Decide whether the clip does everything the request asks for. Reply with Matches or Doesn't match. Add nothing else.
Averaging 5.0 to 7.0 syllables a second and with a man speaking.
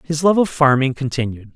Matches